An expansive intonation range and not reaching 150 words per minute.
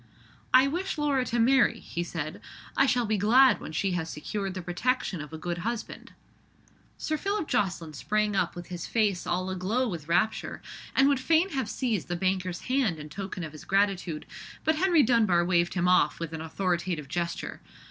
No: wide, 6.5 semitones; average, 190 wpm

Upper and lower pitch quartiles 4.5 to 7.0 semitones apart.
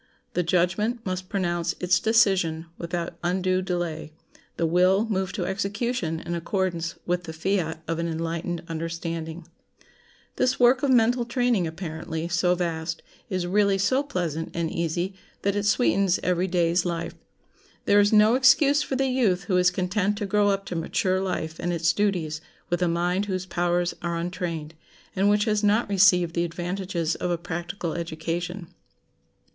No: average, 3.0 semitones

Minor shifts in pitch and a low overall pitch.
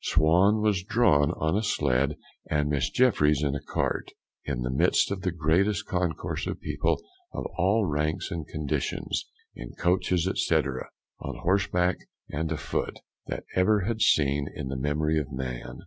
No: average, 4.7 semitones; very low, 80 Hz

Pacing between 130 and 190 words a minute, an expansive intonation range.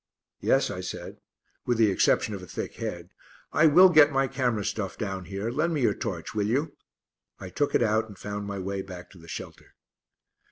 No: fast, 205 wpm; wide, 5.7 semitones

